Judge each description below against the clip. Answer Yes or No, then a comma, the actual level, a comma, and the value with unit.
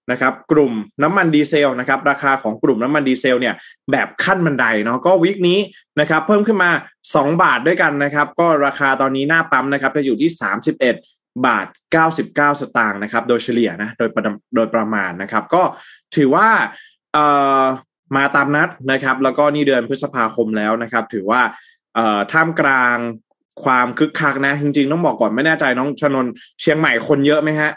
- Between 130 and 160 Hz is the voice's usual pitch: Yes, medium, 140 Hz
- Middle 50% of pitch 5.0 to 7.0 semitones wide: No, average, 4.0 semitones